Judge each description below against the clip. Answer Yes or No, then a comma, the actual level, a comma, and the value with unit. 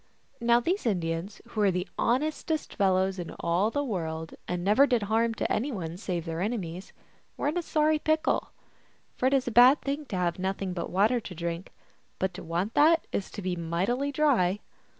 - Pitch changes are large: Yes, wide, 6.5 semitones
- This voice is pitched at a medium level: No, high, 205 Hz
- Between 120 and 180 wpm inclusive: No, average, 195 wpm